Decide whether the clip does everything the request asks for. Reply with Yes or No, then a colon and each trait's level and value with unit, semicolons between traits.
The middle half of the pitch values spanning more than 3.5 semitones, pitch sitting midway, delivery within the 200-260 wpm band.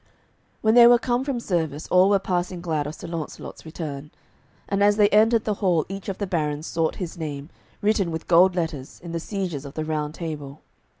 Yes: average, 4.4 semitones; medium, 170 Hz; fast, 205 wpm